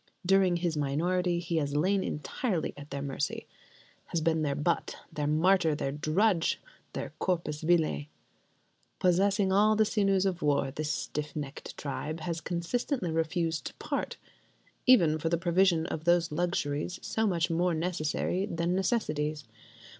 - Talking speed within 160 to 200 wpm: No, average, 145 wpm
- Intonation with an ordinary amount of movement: Yes, average, 3.3 semitones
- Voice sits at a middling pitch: Yes, medium, 170 Hz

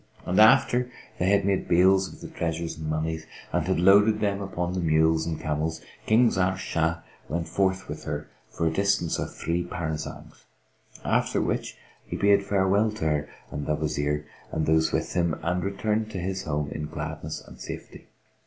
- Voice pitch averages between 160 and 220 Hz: No, very low, 85 Hz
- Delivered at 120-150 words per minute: No, average, 180 wpm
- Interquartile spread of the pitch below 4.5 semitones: Yes, average, 3.7 semitones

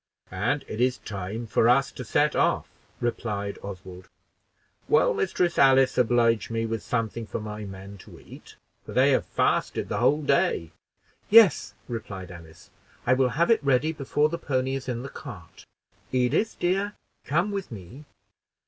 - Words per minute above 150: Yes, average, 160 wpm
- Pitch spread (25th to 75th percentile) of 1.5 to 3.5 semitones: No, average, 5.1 semitones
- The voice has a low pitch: Yes, low, 120 Hz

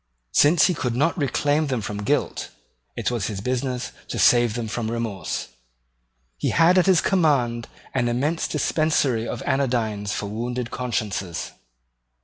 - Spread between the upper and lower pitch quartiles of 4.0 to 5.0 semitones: Yes, average, 4.6 semitones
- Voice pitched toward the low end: Yes, low, 125 Hz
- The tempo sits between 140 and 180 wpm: Yes, average, 145 wpm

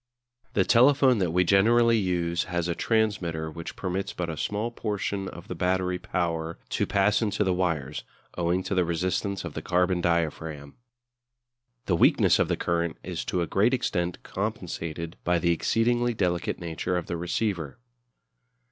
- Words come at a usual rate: Yes, average, 165 wpm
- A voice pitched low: Yes, very low, 90 Hz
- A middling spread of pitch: Yes, average, 3.2 semitones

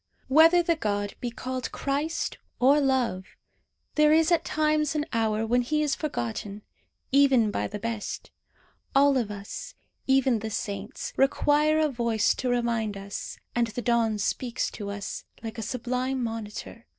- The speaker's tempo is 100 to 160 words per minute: Yes, average, 155 wpm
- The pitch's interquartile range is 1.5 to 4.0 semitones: No, average, 4.6 semitones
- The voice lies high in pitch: Yes, high, 245 Hz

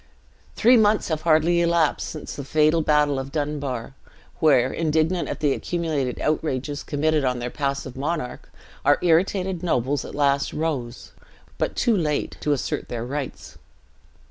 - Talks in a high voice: No, medium, 150 Hz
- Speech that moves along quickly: No, average, 145 wpm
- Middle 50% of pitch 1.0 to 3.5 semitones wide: Yes, average, 2.9 semitones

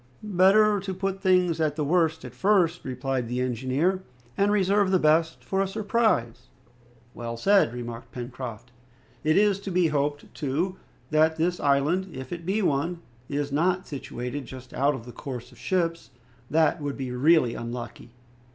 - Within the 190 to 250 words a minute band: No, average, 165 wpm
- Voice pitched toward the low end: No, medium, 155 Hz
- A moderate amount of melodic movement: No, wide, 6.3 semitones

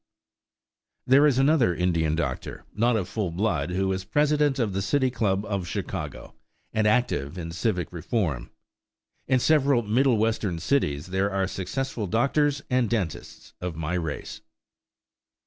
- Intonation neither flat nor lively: No, wide, 6.3 semitones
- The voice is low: Yes, low, 105 Hz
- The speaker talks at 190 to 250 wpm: No, average, 145 wpm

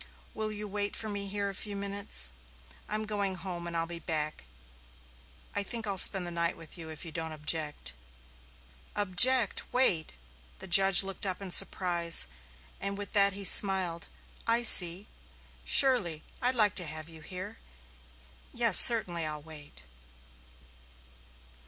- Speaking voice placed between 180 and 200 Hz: Yes, high, 190 Hz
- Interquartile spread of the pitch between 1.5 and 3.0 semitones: No, average, 3.6 semitones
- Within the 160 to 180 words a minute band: No, average, 150 wpm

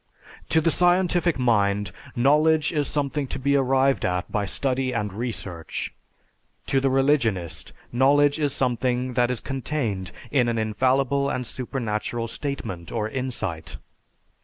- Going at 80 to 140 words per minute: Yes, slow, 135 wpm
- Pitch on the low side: Yes, low, 130 Hz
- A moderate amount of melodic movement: Yes, average, 4.2 semitones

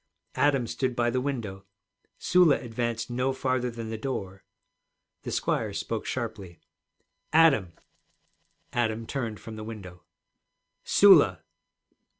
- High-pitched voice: No, low, 120 Hz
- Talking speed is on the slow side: Yes, slow, 115 wpm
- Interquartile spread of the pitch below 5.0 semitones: Yes, average, 3.2 semitones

